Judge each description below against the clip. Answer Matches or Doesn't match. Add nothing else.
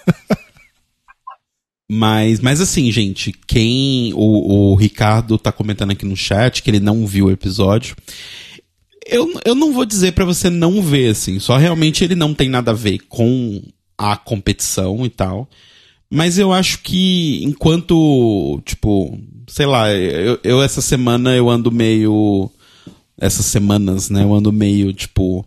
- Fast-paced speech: Doesn't match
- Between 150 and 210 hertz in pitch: Doesn't match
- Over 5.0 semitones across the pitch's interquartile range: Matches